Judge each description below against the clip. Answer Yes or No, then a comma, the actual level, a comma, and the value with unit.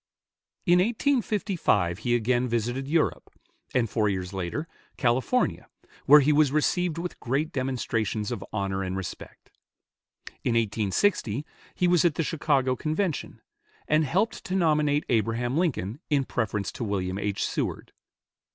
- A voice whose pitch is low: Yes, low, 130 Hz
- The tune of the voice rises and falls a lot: Yes, wide, 6.6 semitones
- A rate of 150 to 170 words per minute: No, slow, 135 wpm